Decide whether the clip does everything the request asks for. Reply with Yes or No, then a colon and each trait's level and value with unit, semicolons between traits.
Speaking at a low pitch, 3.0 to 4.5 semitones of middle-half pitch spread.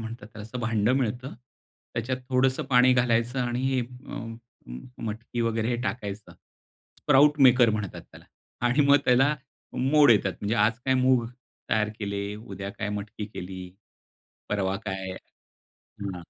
Yes: low, 115 Hz; average, 3.5 semitones